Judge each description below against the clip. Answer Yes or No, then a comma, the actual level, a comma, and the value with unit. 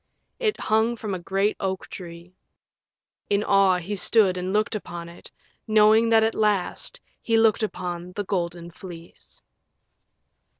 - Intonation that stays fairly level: No, average, 3.4 semitones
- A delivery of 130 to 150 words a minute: Yes, average, 140 wpm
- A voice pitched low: No, high, 195 Hz